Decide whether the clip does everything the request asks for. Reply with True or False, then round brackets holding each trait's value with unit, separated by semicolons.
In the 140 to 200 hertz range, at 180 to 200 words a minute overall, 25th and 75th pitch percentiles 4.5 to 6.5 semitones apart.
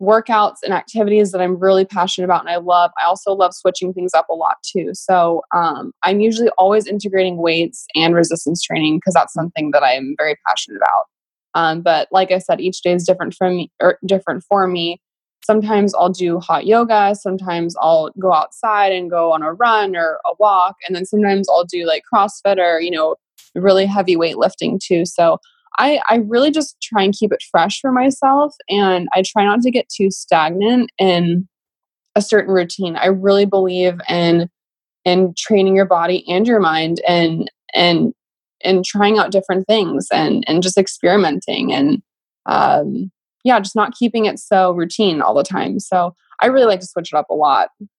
False (185 Hz; 190 wpm; 3.2 semitones)